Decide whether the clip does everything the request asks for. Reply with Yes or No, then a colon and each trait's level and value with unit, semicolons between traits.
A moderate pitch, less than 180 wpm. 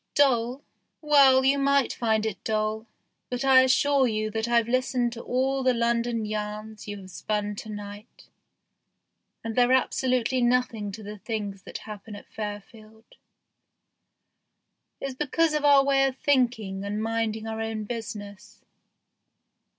No: high, 230 Hz; average, 145 wpm